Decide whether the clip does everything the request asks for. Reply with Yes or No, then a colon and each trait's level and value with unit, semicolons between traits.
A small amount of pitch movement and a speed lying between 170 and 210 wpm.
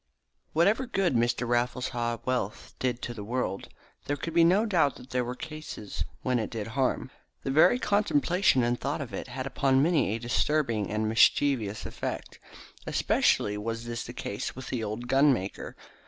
No: average, 4.1 semitones; average, 175 wpm